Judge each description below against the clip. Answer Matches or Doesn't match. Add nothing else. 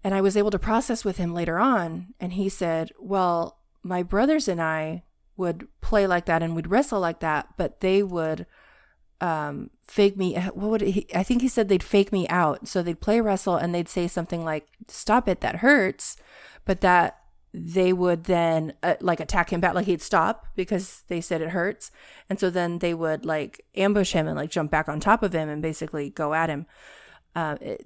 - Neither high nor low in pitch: Matches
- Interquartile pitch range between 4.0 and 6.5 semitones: Doesn't match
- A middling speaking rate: Doesn't match